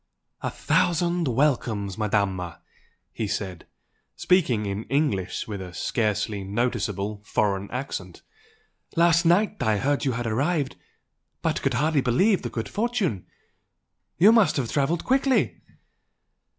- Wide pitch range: Yes, wide, 8.4 semitones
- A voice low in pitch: Yes, low, 125 Hz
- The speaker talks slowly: Yes, slow, 125 wpm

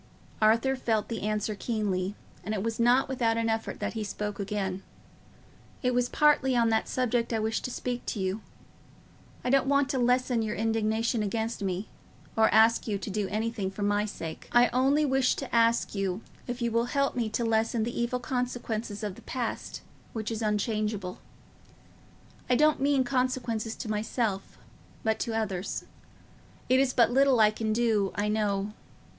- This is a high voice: Yes, high, 225 Hz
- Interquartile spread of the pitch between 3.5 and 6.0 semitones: No, narrow, 2.6 semitones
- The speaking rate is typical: Yes, average, 175 wpm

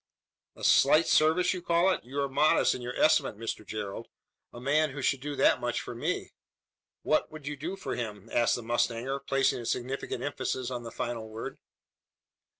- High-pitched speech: No, low, 135 Hz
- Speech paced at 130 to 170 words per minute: No, average, 190 wpm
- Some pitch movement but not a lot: Yes, average, 4.3 semitones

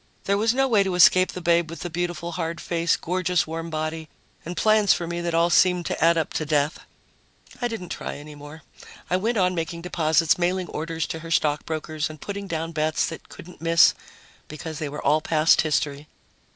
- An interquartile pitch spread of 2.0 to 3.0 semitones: Yes, narrow, 2.4 semitones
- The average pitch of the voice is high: No, medium, 165 Hz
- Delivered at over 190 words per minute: Yes, fast, 205 wpm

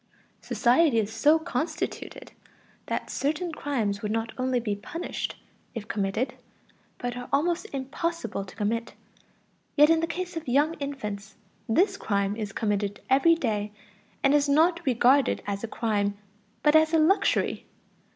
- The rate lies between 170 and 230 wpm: No, average, 145 wpm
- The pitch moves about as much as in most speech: No, wide, 6.8 semitones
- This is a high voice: Yes, very high, 260 Hz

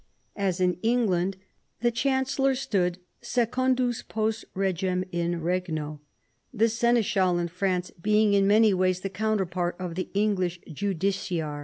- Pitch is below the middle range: No, high, 195 Hz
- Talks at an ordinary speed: No, slow, 130 wpm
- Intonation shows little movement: No, average, 3.8 semitones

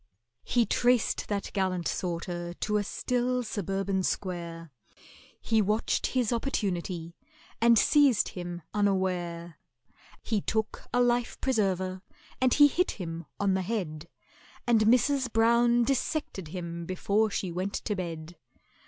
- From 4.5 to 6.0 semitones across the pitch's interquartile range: Yes, average, 5.1 semitones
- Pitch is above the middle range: Yes, high, 200 Hz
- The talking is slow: Yes, slow, 125 wpm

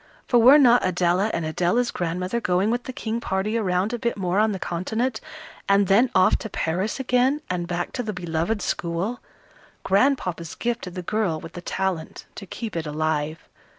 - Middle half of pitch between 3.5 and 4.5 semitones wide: No, average, 5.0 semitones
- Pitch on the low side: No, high, 190 Hz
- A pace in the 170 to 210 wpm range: Yes, average, 185 wpm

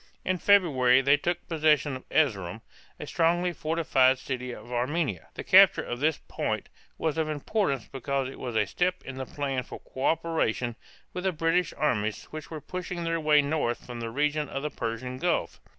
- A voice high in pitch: No, medium, 145 Hz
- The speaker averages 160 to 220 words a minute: Yes, average, 180 wpm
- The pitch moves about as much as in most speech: Yes, average, 4.4 semitones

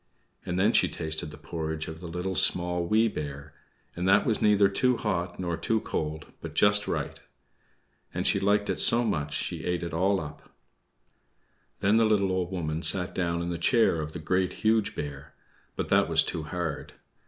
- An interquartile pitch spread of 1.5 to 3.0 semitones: No, average, 4.3 semitones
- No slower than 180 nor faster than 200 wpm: Yes, average, 195 wpm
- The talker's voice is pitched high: No, very low, 90 Hz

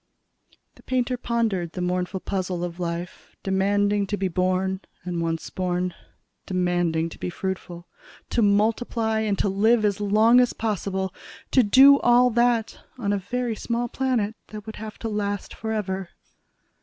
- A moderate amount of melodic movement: Yes, average, 3.6 semitones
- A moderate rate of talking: Yes, average, 155 wpm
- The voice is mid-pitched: No, high, 205 Hz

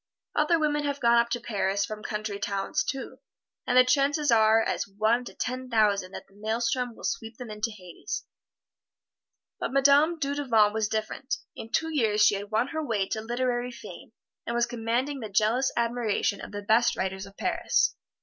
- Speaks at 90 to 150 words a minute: No, average, 185 wpm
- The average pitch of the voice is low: No, high, 230 Hz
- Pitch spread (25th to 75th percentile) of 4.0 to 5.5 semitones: No, average, 3.3 semitones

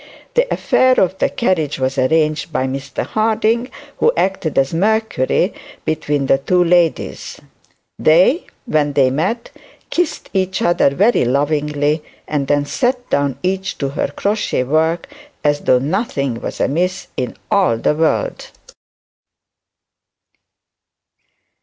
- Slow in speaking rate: Yes, slow, 125 wpm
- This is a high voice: No, medium, 160 Hz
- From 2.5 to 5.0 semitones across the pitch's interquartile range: No, wide, 5.6 semitones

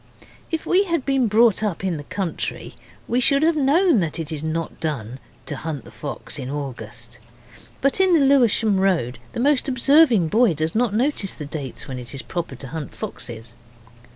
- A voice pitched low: No, high, 190 Hz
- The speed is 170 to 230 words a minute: Yes, average, 190 wpm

